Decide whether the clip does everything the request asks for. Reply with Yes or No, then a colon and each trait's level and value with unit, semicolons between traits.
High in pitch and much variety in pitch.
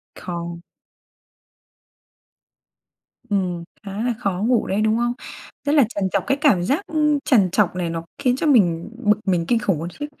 Yes: high, 205 Hz; wide, 6.0 semitones